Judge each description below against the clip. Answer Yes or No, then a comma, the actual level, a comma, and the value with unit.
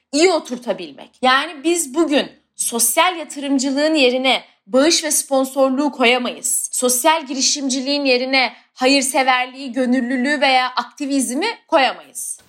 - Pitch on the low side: No, very high, 270 Hz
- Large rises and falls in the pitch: No, average, 2.7 semitones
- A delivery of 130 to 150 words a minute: No, slow, 95 wpm